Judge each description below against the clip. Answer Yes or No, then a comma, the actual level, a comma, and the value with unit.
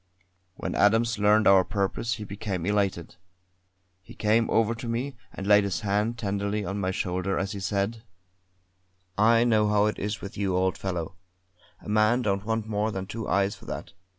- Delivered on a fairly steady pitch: Yes, narrow, 2.0 semitones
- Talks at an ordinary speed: Yes, average, 180 wpm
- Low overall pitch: Yes, low, 105 Hz